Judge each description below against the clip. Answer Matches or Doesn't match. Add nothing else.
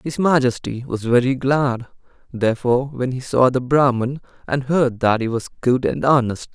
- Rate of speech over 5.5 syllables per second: Doesn't match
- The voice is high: Doesn't match